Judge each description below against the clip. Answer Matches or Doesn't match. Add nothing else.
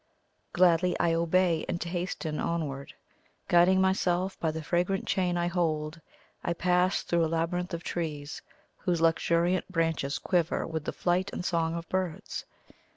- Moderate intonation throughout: Doesn't match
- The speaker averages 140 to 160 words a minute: Matches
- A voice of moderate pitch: Matches